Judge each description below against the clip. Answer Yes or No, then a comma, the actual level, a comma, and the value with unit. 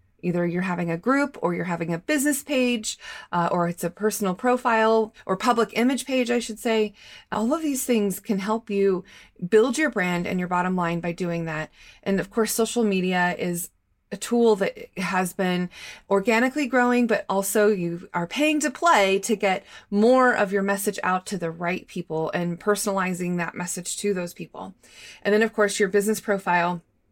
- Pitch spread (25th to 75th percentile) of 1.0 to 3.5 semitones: No, average, 4.2 semitones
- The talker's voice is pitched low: No, high, 200 Hz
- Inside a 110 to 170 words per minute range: No, average, 190 wpm